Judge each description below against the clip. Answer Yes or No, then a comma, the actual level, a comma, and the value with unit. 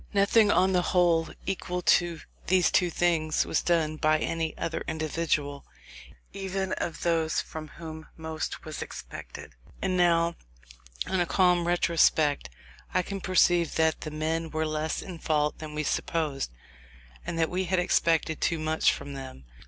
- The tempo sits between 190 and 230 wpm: No, average, 155 wpm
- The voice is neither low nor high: Yes, medium, 165 Hz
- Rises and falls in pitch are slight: Yes, narrow, 2.2 semitones